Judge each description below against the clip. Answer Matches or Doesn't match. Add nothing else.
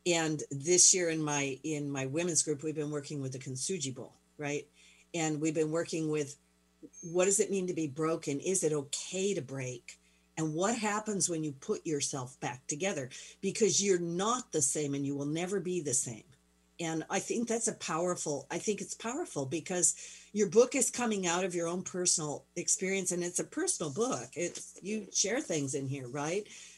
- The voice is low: Doesn't match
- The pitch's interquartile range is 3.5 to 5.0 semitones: Matches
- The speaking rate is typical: Matches